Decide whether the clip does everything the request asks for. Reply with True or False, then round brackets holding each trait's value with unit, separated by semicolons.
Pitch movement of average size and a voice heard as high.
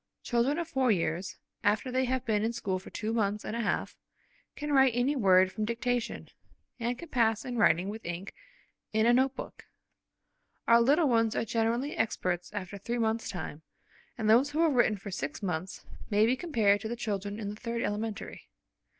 True (3.3 semitones; 225 Hz)